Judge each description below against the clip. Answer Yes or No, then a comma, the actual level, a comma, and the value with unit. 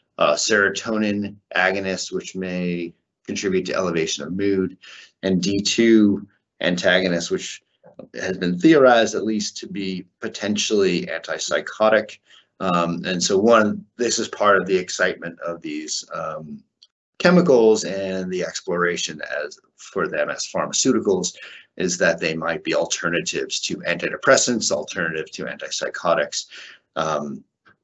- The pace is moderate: No, slow, 125 wpm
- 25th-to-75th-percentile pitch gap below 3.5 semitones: Yes, average, 2.9 semitones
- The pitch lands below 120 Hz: Yes, low, 100 Hz